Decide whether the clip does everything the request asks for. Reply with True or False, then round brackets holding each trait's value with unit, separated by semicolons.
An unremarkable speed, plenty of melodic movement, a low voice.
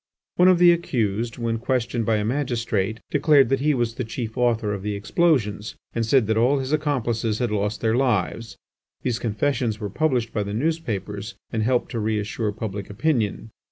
False (185 wpm; 3.6 semitones; 115 Hz)